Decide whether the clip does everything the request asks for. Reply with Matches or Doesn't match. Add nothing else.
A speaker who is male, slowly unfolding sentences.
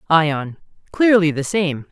Matches